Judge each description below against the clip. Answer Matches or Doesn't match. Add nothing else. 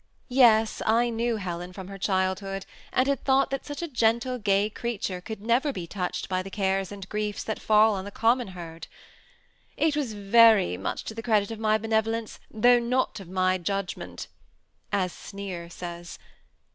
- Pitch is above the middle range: Matches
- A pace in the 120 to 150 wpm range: Doesn't match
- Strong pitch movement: Doesn't match